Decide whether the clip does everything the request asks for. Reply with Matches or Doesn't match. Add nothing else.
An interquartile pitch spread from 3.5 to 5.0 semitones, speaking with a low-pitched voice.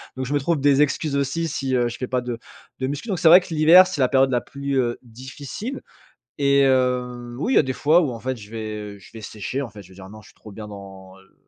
Matches